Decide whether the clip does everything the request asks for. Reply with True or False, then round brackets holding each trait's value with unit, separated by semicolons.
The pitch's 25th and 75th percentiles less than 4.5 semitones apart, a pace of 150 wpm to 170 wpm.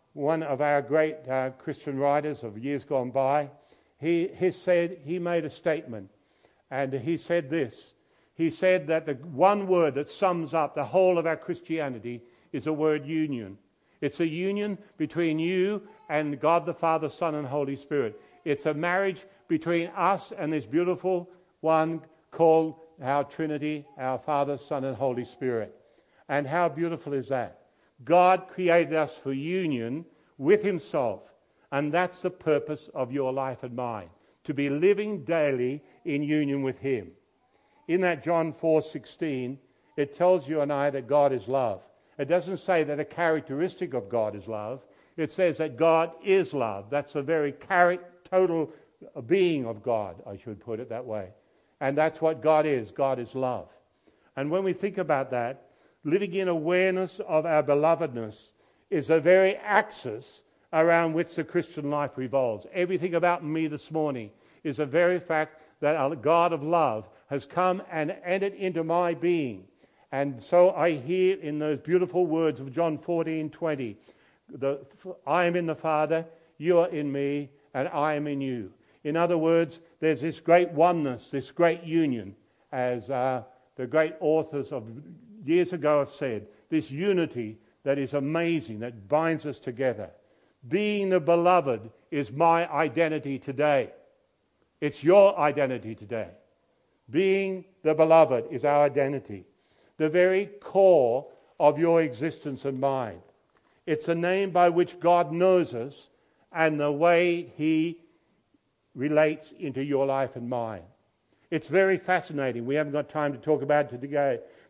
True (3.9 semitones; 160 wpm)